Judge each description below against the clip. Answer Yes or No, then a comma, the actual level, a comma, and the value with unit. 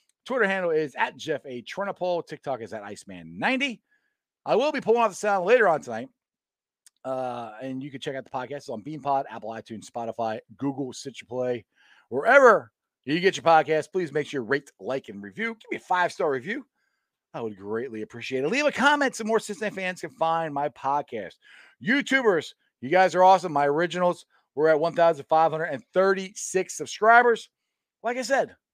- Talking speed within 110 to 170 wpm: No, average, 190 wpm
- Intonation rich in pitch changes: Yes, wide, 8.1 semitones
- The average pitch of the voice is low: No, medium, 160 Hz